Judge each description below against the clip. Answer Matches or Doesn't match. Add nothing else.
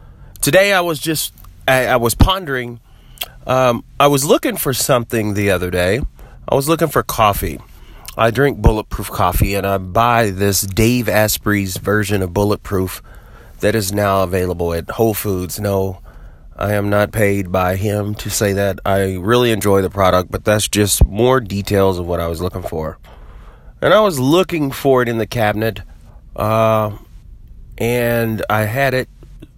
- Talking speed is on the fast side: Doesn't match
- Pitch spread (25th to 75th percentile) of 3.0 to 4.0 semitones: Matches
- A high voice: Doesn't match